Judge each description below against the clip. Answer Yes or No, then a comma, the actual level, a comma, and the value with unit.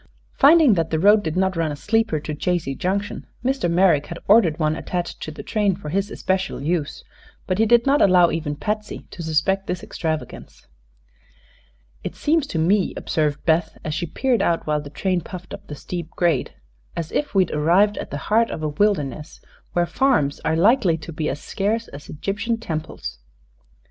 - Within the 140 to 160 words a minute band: No, average, 190 wpm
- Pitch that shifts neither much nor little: Yes, average, 4.7 semitones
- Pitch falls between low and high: Yes, medium, 175 Hz